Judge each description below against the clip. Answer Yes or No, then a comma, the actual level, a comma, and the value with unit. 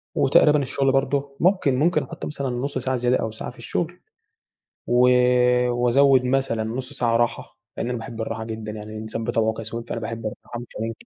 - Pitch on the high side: No, low, 120 Hz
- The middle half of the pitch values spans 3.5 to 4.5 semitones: No, average, 3.1 semitones